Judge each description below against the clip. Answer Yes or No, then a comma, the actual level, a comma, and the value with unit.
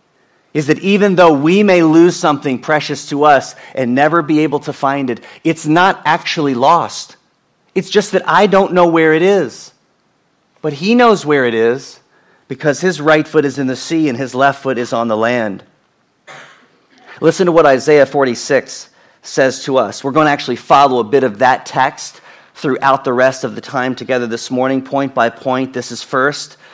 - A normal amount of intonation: Yes, average, 4.0 semitones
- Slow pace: No, average, 195 wpm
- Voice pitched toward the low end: No, medium, 145 Hz